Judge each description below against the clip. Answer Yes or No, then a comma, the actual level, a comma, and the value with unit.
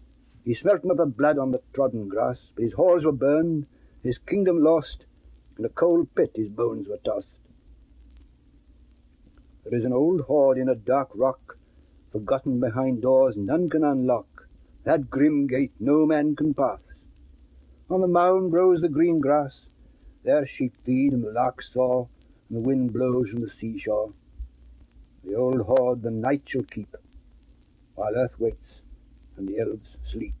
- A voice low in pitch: Yes, low, 125 Hz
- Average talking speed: Yes, average, 160 wpm